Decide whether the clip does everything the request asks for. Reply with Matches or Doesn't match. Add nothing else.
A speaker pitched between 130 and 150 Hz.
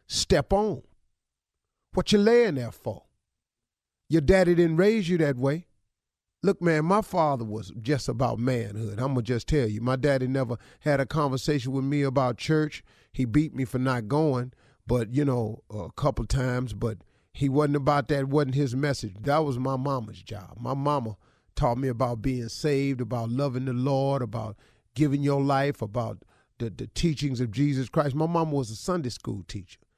Matches